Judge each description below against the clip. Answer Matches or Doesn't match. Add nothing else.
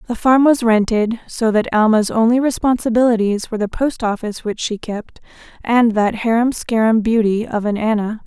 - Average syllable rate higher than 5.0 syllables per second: Matches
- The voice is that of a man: Doesn't match